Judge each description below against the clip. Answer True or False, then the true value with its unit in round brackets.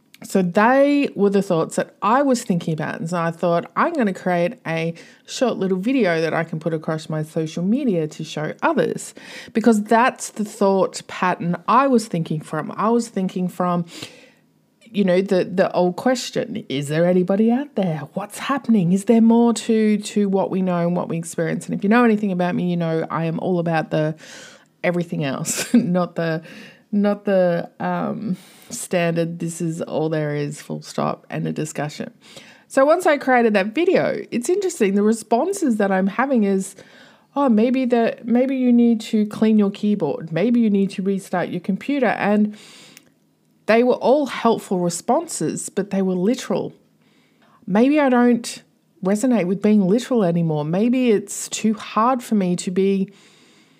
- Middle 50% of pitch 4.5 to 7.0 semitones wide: True (5.0 semitones)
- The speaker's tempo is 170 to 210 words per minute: True (180 wpm)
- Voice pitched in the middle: False (200 Hz)